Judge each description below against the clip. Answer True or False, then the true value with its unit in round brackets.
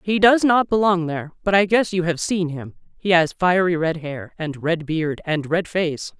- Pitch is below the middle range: False (175 Hz)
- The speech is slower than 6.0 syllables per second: True (4.6 syllables/s)